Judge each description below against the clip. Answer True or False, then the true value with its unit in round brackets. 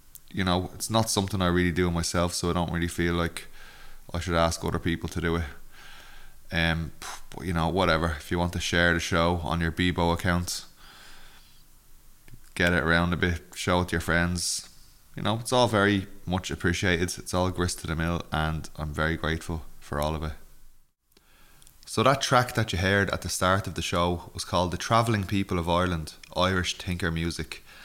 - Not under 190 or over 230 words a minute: True (200 wpm)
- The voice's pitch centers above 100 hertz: False (85 Hz)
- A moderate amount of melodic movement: False (1.5 semitones)